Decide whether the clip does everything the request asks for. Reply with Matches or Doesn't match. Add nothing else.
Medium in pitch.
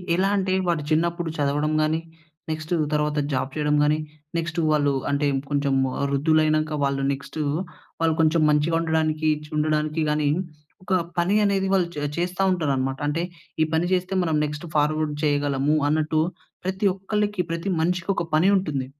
Matches